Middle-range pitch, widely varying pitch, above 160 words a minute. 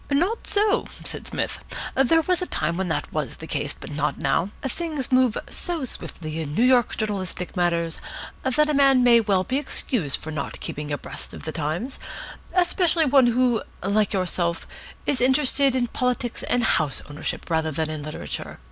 No: high, 240 Hz; wide, 8.4 semitones; average, 175 wpm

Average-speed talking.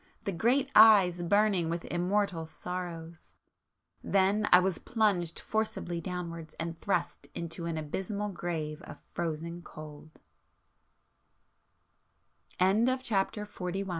No: slow, 95 wpm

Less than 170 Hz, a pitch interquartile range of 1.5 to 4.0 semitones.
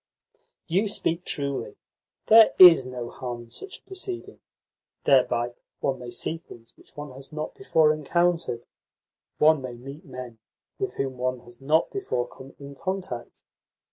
No: medium, 140 Hz; wide, 5.5 semitones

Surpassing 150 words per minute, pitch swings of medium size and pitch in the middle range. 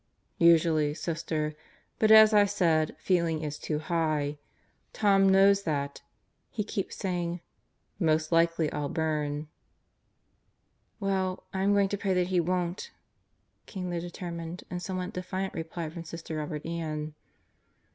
No: slow, 135 wpm; average, 3.2 semitones; medium, 170 Hz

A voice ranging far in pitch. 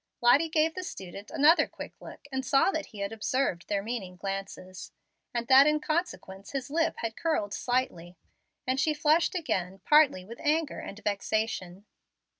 Yes: wide, 7.4 semitones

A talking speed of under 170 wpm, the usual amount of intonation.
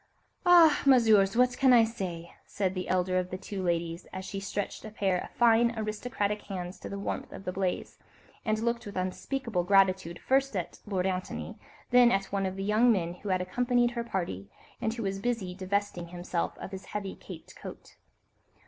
No: average, 195 wpm; average, 4.0 semitones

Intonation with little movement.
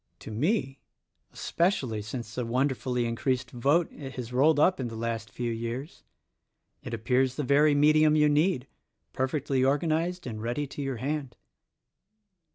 No: average, 3.8 semitones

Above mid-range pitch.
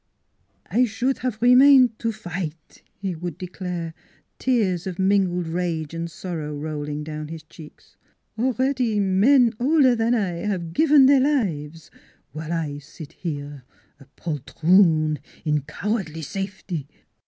No: medium, 180 Hz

